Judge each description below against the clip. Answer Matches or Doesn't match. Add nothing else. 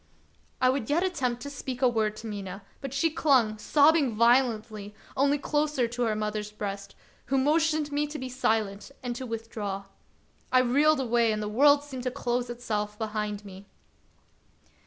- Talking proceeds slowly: Doesn't match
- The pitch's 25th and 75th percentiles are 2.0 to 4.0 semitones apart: Doesn't match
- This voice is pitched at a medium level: Doesn't match